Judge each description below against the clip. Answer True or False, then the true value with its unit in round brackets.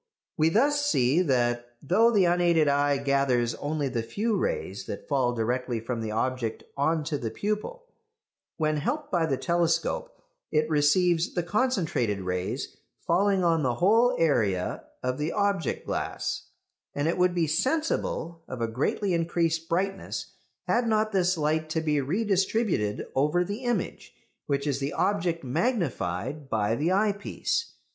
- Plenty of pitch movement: True (6.6 semitones)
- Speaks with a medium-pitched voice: True (160 Hz)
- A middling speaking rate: True (150 wpm)